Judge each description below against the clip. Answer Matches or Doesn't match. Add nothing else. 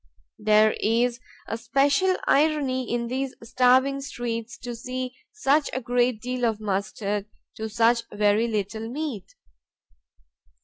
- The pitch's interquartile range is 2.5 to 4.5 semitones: Matches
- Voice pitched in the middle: Doesn't match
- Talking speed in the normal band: Doesn't match